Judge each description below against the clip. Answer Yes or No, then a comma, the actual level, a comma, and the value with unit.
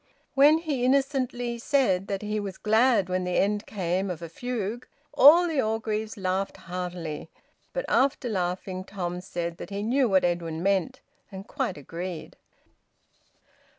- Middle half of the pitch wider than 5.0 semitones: Yes, wide, 5.4 semitones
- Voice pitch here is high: Yes, high, 200 Hz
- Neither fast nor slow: Yes, average, 150 wpm